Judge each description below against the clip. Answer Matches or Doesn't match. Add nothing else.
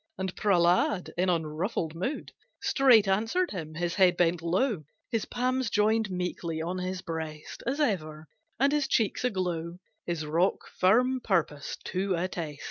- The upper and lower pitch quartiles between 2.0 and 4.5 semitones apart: Doesn't match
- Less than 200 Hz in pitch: Matches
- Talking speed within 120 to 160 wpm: Matches